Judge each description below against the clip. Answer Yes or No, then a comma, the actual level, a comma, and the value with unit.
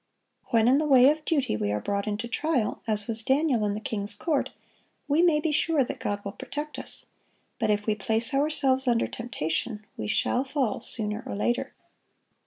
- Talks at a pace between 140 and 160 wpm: No, average, 195 wpm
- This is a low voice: No, high, 235 Hz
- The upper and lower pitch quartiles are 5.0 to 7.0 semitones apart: Yes, wide, 5.4 semitones